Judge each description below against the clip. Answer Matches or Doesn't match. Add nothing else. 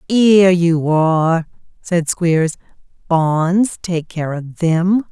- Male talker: Doesn't match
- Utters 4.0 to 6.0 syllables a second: Doesn't match